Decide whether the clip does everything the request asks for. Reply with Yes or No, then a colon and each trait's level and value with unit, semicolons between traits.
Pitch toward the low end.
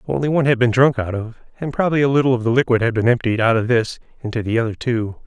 Yes: low, 120 Hz